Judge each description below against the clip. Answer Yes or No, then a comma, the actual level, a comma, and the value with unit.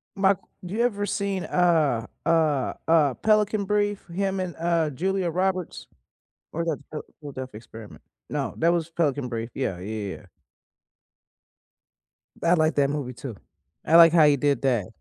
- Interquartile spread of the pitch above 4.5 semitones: Yes, wide, 5.6 semitones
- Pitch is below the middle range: No, medium, 165 Hz